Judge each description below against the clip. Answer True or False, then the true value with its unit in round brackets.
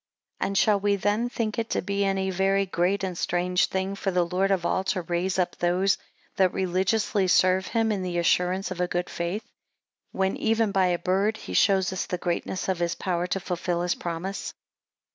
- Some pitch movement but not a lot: False (1.8 semitones)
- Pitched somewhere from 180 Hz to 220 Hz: True (190 Hz)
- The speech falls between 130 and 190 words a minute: False (205 wpm)